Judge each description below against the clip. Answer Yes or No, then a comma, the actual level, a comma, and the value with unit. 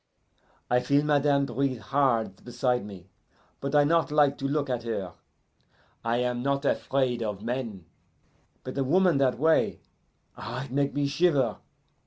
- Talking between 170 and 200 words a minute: No, average, 155 wpm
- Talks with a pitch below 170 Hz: Yes, low, 135 Hz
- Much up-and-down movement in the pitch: No, average, 3.1 semitones